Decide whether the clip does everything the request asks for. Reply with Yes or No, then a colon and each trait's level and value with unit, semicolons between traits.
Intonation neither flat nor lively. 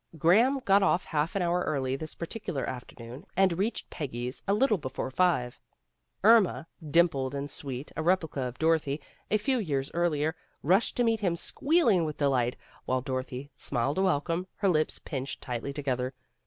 No: wide, 5.9 semitones